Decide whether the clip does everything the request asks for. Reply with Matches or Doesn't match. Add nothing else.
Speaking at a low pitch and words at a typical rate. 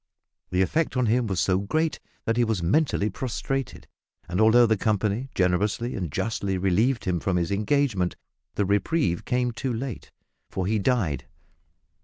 Matches